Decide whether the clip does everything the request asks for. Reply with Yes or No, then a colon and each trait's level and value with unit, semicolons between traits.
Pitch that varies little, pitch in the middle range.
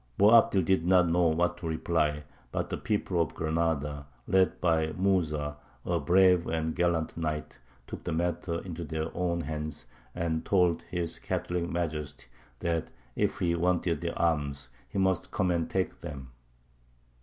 No: narrow, 2.1 semitones; very low, 85 Hz